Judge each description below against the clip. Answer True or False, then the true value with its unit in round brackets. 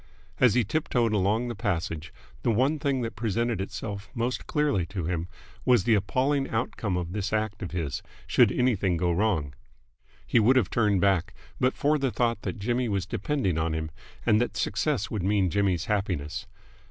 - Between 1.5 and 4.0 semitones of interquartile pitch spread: False (4.6 semitones)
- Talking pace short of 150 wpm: False (185 wpm)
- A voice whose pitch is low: True (105 Hz)